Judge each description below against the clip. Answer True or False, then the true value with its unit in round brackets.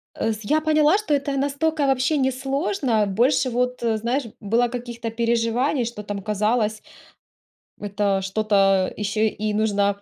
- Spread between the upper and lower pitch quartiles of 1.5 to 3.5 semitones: False (4.3 semitones)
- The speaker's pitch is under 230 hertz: False (235 Hz)